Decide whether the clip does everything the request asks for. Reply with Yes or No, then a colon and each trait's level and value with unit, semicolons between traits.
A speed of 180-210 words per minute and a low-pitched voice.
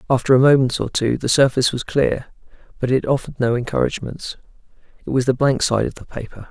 Yes: fast, 205 wpm; low, 125 Hz